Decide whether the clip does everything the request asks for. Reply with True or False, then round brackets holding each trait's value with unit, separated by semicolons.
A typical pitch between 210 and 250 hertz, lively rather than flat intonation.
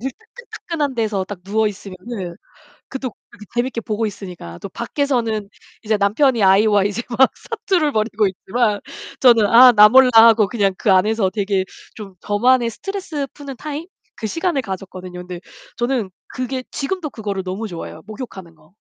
False (220 Hz; 4.7 semitones)